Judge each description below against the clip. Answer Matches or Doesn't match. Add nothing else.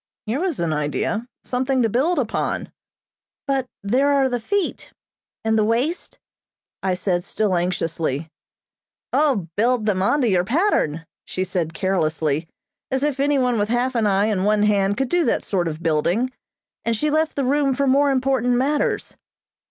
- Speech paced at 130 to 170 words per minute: Matches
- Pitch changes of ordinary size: Doesn't match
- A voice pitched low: Doesn't match